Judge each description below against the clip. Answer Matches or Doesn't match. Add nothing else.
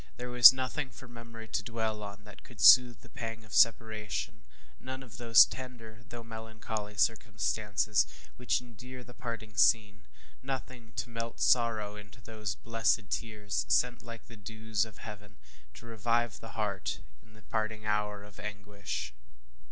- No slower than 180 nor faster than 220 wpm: Doesn't match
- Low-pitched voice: Matches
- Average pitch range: Doesn't match